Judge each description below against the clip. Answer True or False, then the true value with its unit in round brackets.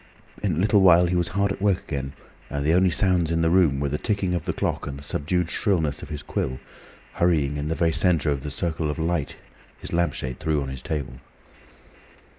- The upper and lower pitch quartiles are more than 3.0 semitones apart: True (3.7 semitones)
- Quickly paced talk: True (225 wpm)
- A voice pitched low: True (80 Hz)